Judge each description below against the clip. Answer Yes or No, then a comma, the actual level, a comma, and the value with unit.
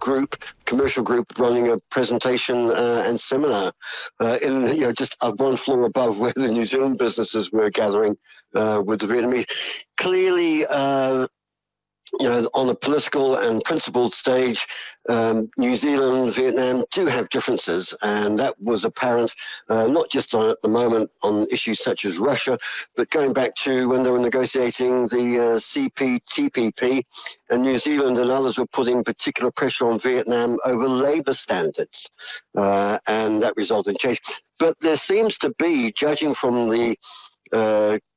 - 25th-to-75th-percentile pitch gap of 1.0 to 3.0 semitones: Yes, narrow, 2.6 semitones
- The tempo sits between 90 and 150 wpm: No, average, 160 wpm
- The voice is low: Yes, low, 125 Hz